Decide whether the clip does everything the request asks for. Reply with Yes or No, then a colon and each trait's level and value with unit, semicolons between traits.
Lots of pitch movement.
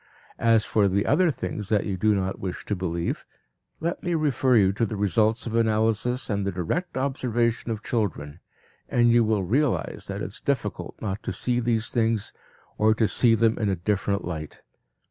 No: average, 3.2 semitones